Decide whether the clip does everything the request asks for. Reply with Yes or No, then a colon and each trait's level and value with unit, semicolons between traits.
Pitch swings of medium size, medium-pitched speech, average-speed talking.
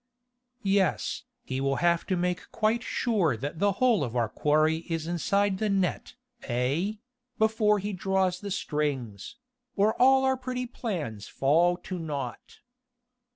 No: wide, 6.0 semitones; medium, 180 Hz; average, 145 wpm